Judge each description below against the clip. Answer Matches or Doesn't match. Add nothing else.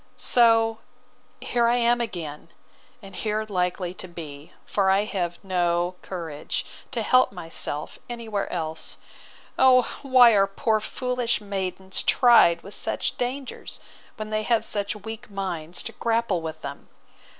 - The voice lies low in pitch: Doesn't match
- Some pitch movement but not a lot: Matches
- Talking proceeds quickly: Doesn't match